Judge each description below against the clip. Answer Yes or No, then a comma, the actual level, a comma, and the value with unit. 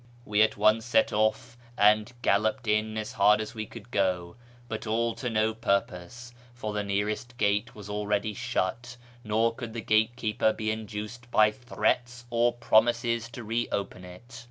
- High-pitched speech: No, low, 110 Hz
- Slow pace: No, average, 165 wpm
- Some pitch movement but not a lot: No, narrow, 2.2 semitones